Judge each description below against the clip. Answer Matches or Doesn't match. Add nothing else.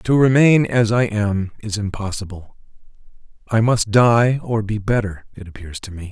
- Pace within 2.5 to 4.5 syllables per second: Doesn't match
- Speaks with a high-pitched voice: Doesn't match